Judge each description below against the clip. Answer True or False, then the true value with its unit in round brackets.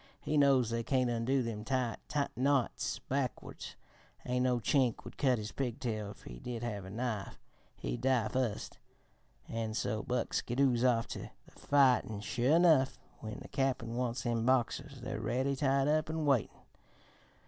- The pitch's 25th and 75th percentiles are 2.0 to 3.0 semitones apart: True (2.7 semitones)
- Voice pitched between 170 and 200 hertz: False (125 Hz)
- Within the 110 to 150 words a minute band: False (165 wpm)